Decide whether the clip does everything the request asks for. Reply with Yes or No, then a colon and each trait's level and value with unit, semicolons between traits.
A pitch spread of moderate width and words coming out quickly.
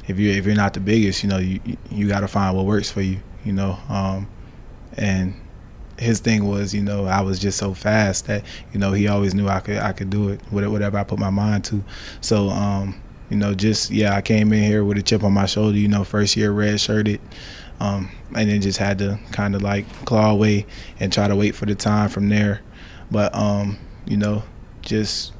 No: narrow, 1.2 semitones; fast, 230 wpm